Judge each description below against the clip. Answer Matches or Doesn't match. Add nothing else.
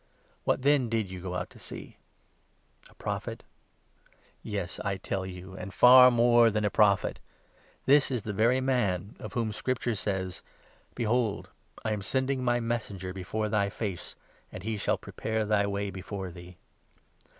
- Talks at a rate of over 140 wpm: Matches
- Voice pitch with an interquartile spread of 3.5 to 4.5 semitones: Matches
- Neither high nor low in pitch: Doesn't match